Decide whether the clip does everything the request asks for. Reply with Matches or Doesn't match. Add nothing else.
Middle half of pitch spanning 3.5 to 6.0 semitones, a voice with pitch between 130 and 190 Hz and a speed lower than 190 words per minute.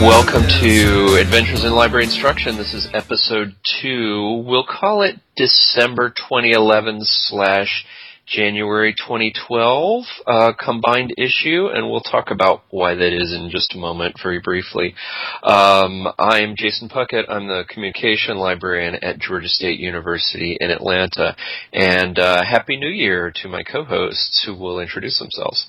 Doesn't match